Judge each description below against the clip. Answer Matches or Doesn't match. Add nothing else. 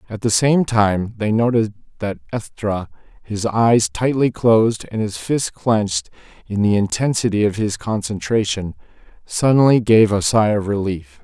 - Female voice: Doesn't match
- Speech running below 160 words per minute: Matches